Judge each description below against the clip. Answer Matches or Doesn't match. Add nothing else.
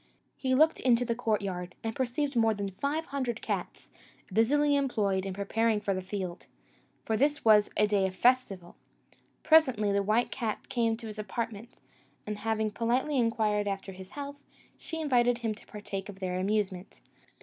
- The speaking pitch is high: Matches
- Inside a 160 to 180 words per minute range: Matches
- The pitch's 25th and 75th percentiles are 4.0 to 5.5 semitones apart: Doesn't match